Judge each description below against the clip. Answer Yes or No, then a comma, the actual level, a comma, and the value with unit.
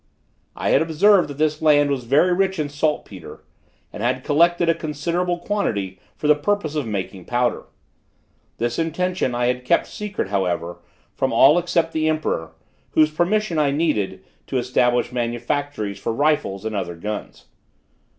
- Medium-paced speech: Yes, average, 155 wpm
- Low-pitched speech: No, medium, 145 Hz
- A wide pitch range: Yes, wide, 5.8 semitones